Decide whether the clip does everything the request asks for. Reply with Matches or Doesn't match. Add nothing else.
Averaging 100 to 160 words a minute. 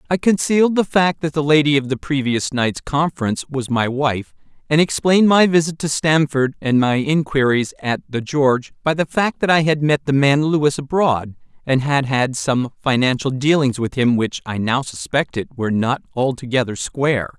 Doesn't match